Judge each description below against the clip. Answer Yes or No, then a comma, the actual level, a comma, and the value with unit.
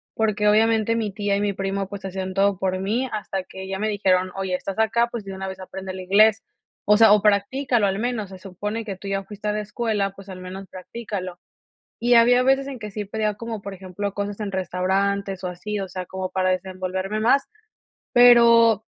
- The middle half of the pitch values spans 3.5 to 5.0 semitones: No, narrow, 2.4 semitones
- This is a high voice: Yes, high, 200 Hz